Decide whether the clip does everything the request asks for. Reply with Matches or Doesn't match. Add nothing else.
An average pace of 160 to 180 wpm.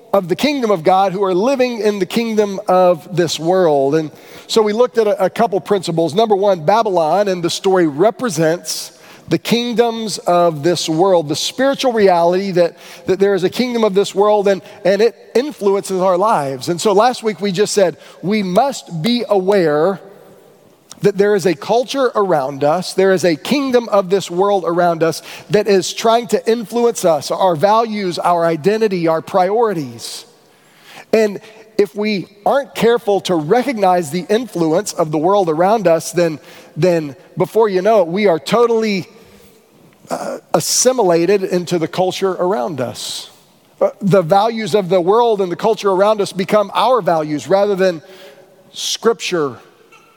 Matches